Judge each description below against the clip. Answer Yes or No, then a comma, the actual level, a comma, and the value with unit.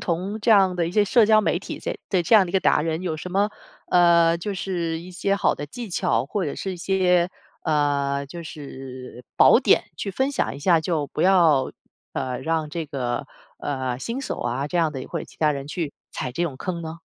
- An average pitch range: Yes, average, 4.7 semitones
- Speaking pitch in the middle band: Yes, medium, 170 Hz